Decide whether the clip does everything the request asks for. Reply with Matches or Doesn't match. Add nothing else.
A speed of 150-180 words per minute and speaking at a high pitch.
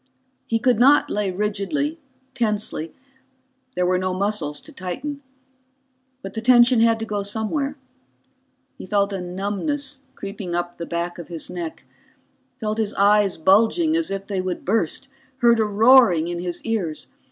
Matches